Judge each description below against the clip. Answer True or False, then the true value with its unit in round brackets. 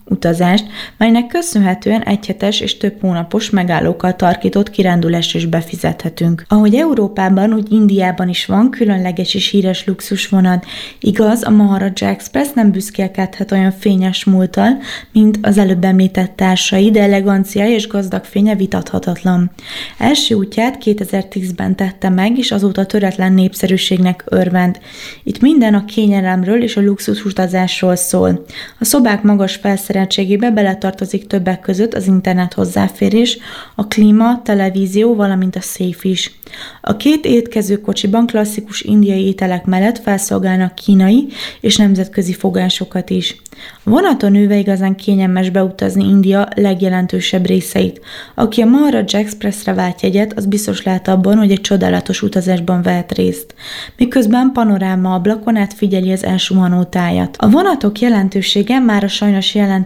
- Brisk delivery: False (130 wpm)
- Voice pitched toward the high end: True (195 Hz)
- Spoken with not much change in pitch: True (2.3 semitones)